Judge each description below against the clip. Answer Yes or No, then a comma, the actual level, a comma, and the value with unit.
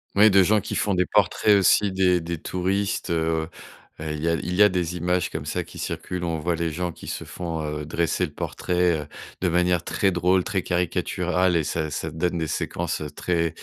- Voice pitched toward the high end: No, very low, 90 Hz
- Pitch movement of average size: No, narrow, 1.9 semitones